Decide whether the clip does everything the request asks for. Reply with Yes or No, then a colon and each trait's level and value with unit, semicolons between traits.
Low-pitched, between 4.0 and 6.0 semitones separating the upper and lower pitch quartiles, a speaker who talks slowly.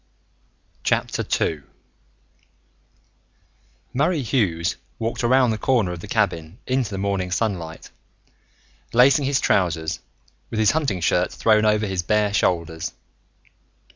Yes: low, 105 Hz; wide, 5.5 semitones; slow, 110 wpm